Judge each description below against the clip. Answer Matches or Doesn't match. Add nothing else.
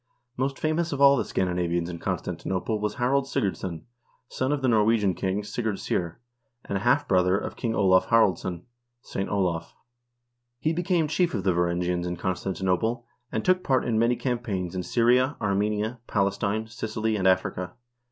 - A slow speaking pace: Doesn't match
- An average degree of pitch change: Matches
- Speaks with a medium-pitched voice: Doesn't match